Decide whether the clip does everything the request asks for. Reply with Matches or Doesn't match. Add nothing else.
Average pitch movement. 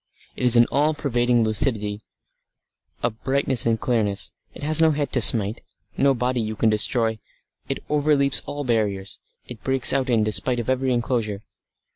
Matches